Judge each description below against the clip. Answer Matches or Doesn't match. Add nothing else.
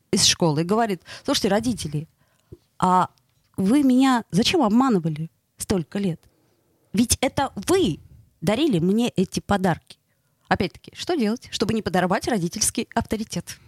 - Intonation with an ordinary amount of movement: Doesn't match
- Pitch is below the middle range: Doesn't match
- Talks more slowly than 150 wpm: Matches